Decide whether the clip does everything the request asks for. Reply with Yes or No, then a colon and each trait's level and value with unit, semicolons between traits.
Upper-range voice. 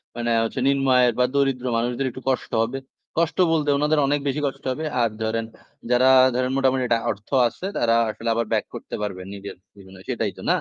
No: low, 125 Hz